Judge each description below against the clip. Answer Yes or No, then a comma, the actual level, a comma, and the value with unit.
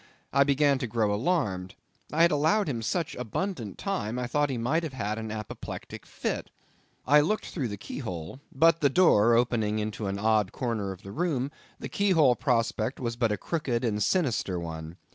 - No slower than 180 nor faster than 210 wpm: Yes, average, 195 wpm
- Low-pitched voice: Yes, low, 120 Hz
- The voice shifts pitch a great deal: Yes, wide, 5.8 semitones